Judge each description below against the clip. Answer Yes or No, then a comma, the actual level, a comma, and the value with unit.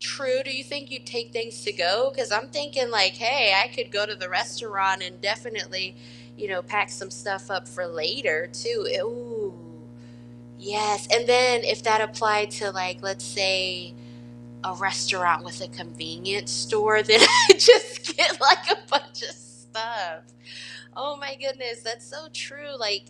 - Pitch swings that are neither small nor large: No, wide, 5.8 semitones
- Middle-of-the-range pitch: No, high, 215 Hz